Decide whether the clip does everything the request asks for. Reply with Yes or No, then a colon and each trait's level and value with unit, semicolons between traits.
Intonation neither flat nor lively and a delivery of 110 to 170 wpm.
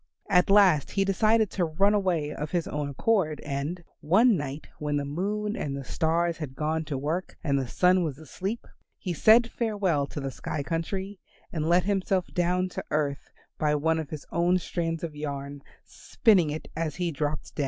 No: average, 4.1 semitones; average, 190 wpm